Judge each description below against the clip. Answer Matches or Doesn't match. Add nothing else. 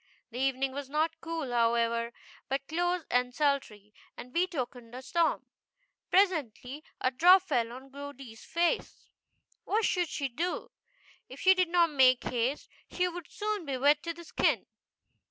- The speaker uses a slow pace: Doesn't match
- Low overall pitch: Doesn't match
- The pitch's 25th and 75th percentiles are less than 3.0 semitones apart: Doesn't match